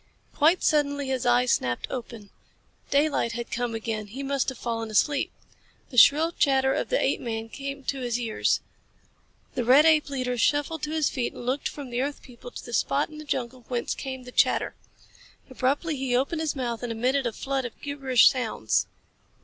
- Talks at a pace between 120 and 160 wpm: No, average, 190 wpm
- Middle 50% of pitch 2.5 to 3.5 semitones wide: Yes, average, 3.0 semitones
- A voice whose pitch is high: Yes, very high, 260 Hz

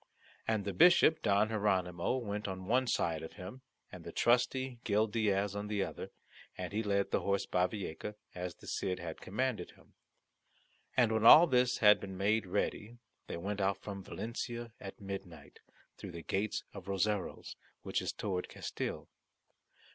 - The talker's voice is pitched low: Yes, low, 100 Hz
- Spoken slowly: No, average, 165 wpm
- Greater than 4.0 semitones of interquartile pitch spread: No, average, 2.9 semitones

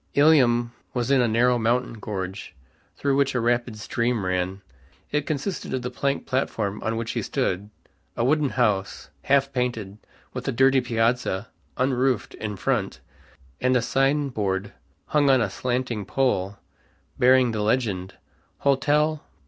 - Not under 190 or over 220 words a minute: No, average, 150 wpm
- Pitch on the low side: Yes, low, 125 Hz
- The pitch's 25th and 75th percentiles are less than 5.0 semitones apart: Yes, average, 4.0 semitones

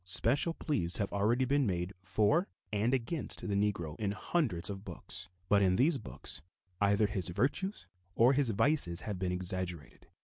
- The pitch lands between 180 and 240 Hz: No, low, 100 Hz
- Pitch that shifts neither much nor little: No, wide, 6.0 semitones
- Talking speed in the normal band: Yes, average, 165 wpm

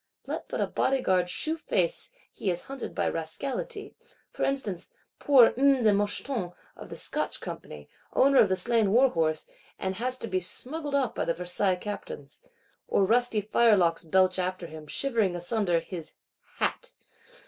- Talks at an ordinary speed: Yes, average, 150 wpm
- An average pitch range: No, wide, 6.1 semitones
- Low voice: No, high, 205 Hz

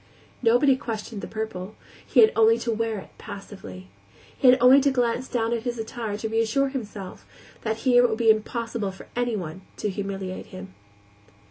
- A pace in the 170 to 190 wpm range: Yes, average, 175 wpm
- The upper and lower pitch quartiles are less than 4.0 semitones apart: Yes, average, 3.1 semitones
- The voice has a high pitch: Yes, high, 225 Hz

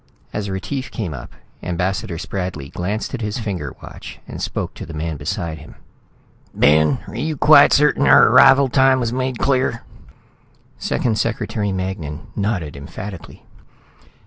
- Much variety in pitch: Yes, wide, 7.3 semitones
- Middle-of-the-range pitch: No, low, 100 Hz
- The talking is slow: No, average, 145 wpm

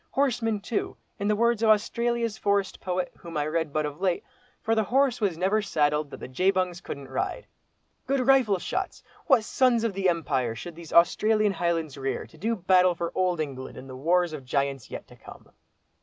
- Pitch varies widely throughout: Yes, wide, 6.0 semitones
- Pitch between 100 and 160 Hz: No, medium, 185 Hz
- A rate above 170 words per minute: Yes, average, 200 wpm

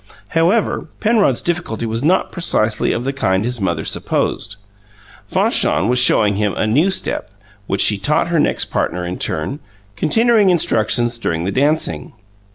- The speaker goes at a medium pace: Yes, average, 155 wpm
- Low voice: Yes, low, 120 Hz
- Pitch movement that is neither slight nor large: No, wide, 8.4 semitones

